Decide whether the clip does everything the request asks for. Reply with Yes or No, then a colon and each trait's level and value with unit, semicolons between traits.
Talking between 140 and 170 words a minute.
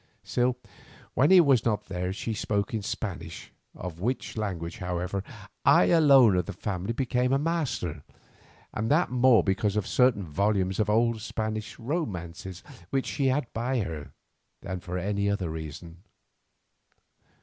Yes: average, 145 wpm